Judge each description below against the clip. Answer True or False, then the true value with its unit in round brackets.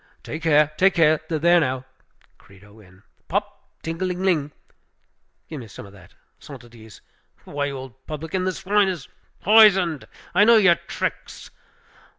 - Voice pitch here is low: False (155 Hz)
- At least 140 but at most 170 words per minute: True (160 wpm)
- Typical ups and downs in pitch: False (6.0 semitones)